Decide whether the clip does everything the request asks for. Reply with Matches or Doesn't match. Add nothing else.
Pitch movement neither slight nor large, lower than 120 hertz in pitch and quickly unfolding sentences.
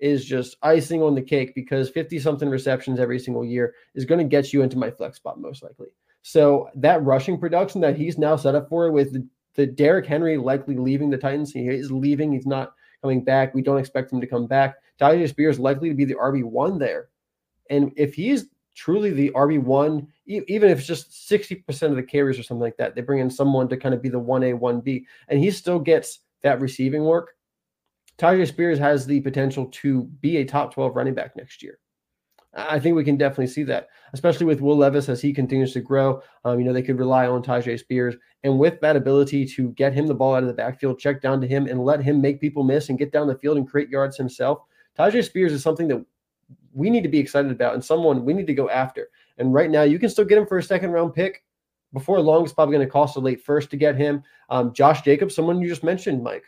Doesn't match